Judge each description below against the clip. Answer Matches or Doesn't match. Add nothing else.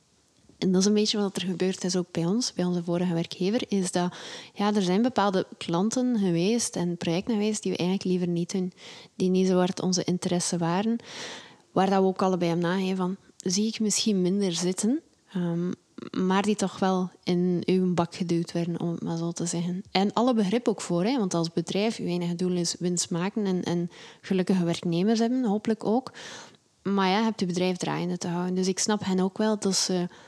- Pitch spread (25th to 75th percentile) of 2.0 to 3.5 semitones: Matches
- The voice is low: Doesn't match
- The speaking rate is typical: Doesn't match